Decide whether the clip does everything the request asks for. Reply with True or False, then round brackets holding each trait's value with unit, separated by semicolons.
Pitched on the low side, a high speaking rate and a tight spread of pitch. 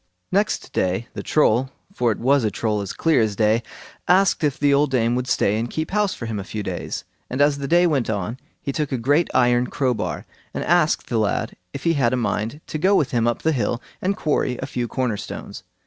False (130 Hz; 225 wpm; 4.7 semitones)